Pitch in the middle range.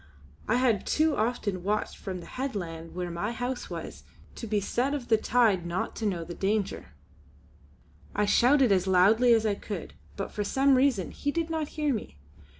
No: high, 215 Hz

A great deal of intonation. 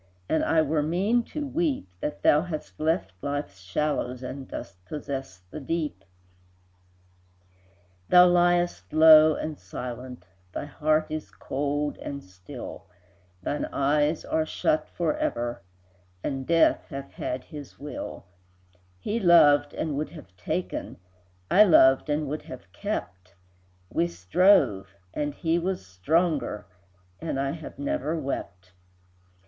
No: average, 4.4 semitones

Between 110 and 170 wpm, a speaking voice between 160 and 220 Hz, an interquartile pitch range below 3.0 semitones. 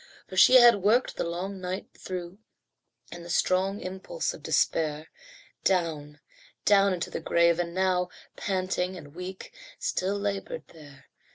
Yes: average, 145 wpm; medium, 185 Hz; narrow, 2.6 semitones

